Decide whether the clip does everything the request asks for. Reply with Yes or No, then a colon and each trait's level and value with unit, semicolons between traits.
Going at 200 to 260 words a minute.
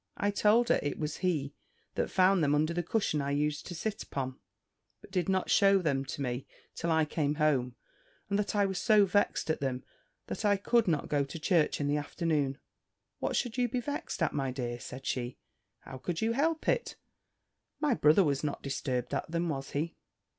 Yes: fast, 205 wpm